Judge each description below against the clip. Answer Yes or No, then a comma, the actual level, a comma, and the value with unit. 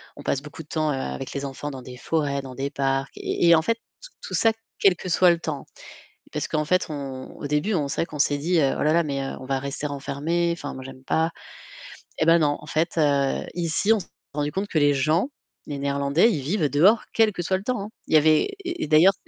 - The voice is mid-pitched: Yes, medium, 150 Hz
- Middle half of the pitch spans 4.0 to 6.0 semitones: No, average, 3.5 semitones